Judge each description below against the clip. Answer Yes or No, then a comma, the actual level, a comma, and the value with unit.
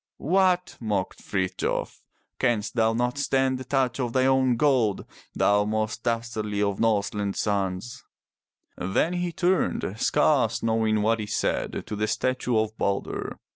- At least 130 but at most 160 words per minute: Yes, average, 140 wpm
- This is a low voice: Yes, low, 115 Hz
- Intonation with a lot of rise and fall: No, average, 3.9 semitones